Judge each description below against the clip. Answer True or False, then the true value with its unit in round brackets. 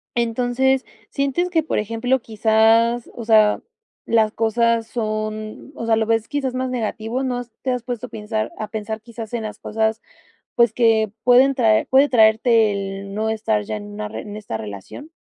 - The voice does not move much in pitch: True (2.3 semitones)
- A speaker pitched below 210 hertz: False (225 Hz)